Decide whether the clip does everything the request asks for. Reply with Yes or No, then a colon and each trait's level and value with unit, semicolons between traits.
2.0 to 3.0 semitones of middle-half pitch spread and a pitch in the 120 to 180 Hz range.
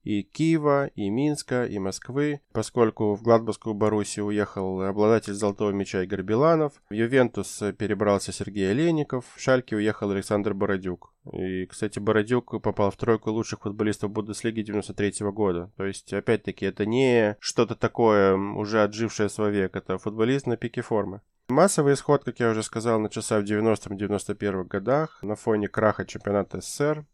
No: narrow, 2.5 semitones; low, 105 Hz